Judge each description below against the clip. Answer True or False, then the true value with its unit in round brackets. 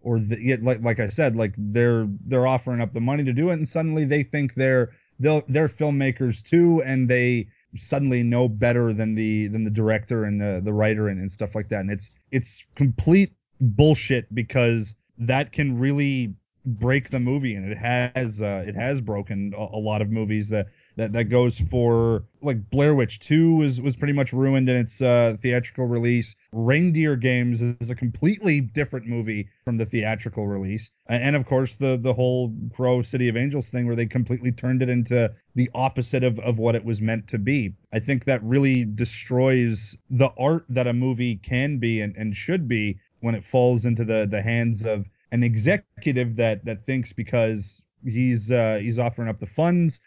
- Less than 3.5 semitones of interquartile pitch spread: True (3.0 semitones)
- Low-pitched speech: True (120 Hz)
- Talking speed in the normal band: True (195 wpm)